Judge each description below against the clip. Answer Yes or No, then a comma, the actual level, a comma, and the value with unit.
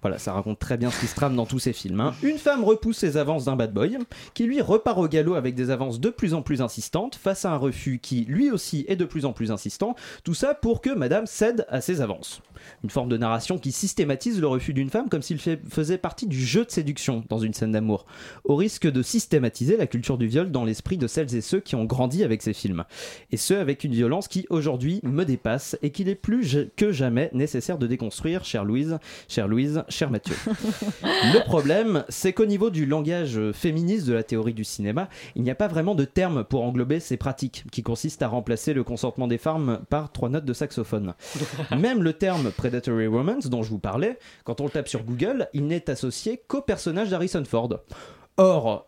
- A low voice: No, medium, 145 Hz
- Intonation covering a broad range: Yes, wide, 7.2 semitones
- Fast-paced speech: Yes, fast, 225 wpm